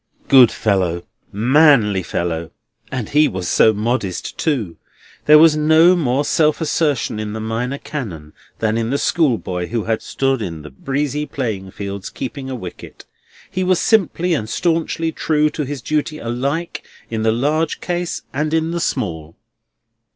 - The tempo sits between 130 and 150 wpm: No, average, 160 wpm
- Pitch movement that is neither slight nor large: No, wide, 6.4 semitones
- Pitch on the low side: Yes, low, 130 Hz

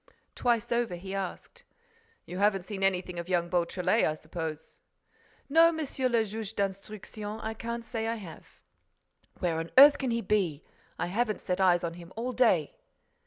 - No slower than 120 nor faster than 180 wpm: Yes, average, 165 wpm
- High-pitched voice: Yes, high, 200 Hz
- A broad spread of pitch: No, average, 4.6 semitones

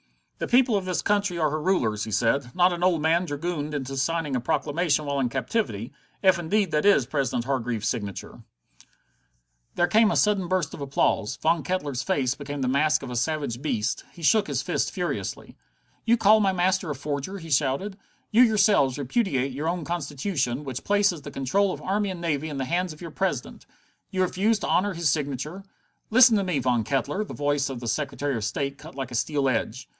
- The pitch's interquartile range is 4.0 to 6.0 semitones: Yes, wide, 5.5 semitones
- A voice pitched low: No, medium, 150 Hz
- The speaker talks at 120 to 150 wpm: No, fast, 205 wpm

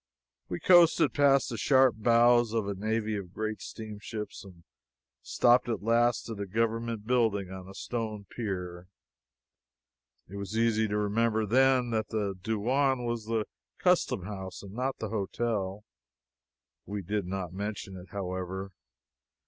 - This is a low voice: Yes, low, 110 Hz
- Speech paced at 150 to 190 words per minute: No, average, 140 wpm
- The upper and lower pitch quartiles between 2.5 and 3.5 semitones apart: Yes, average, 3.0 semitones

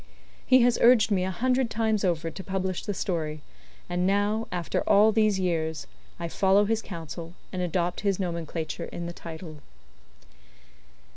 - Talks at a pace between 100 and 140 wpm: No, average, 155 wpm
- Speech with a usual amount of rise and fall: Yes, average, 3.8 semitones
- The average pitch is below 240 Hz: Yes, medium, 185 Hz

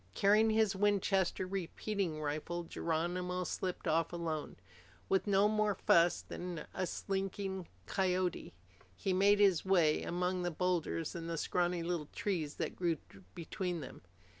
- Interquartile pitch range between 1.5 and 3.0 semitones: Yes, narrow, 2.5 semitones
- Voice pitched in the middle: Yes, medium, 180 Hz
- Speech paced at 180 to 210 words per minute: No, average, 140 wpm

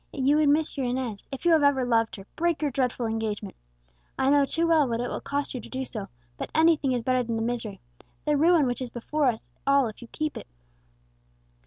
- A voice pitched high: Yes, very high, 260 Hz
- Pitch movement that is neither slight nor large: Yes, average, 4.0 semitones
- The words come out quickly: Yes, fast, 235 wpm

